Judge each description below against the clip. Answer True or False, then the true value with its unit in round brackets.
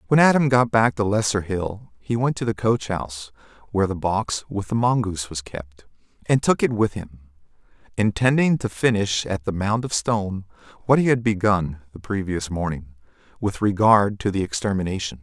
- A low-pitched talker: True (105 Hz)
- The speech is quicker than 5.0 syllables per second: True (5.2 syllables/s)